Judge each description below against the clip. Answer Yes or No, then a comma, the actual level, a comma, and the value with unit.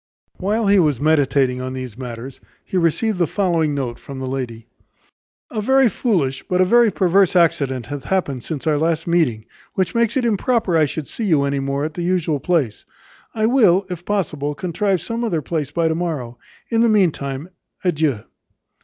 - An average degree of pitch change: No, wide, 5.7 semitones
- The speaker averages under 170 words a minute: No, average, 185 wpm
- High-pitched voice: No, medium, 165 Hz